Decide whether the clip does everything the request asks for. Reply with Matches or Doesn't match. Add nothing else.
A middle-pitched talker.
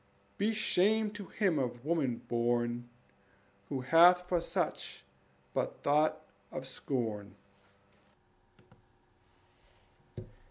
Matches